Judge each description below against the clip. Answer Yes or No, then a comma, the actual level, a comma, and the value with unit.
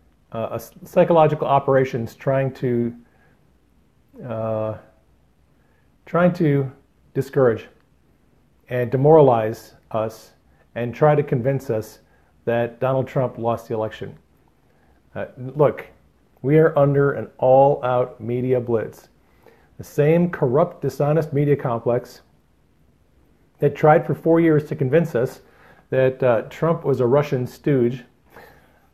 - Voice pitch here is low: Yes, low, 130 Hz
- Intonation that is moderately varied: Yes, average, 3.9 semitones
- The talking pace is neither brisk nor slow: No, slow, 110 wpm